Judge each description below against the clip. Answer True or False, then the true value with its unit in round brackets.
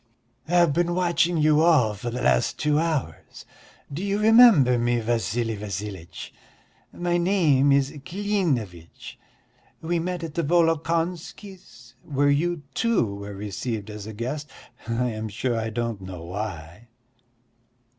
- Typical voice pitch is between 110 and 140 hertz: True (135 Hz)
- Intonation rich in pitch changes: True (7.8 semitones)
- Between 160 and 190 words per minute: False (135 wpm)